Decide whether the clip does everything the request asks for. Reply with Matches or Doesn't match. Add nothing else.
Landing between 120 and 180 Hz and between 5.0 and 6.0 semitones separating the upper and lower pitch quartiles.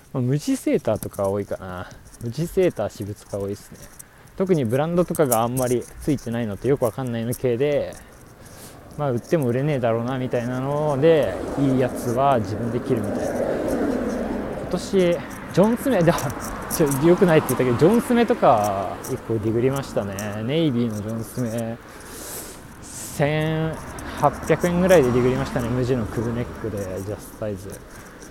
Matches